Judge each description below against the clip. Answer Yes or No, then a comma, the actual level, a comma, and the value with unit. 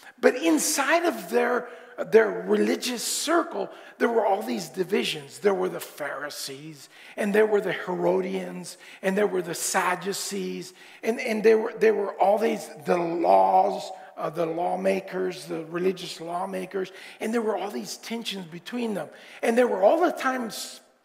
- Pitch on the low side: No, high, 190 Hz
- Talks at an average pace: Yes, average, 160 wpm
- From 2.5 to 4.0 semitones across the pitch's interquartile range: No, average, 4.7 semitones